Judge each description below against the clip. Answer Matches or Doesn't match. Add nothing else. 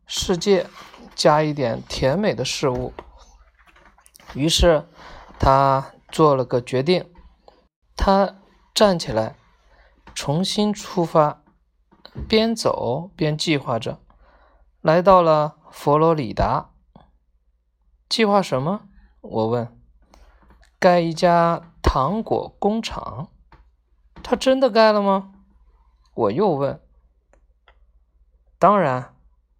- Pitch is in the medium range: Matches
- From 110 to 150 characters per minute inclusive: Matches